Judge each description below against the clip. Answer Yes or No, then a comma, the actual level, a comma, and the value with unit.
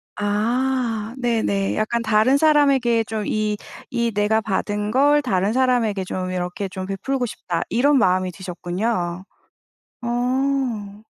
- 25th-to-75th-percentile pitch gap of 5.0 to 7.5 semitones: No, average, 4.3 semitones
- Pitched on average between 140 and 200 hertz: No, high, 220 Hz